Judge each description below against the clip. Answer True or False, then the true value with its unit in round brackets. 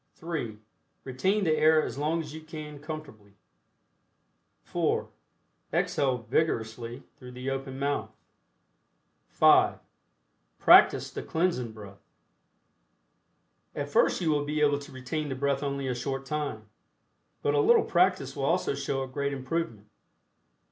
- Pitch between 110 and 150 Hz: True (140 Hz)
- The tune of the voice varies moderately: True (3.2 semitones)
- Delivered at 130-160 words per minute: True (135 wpm)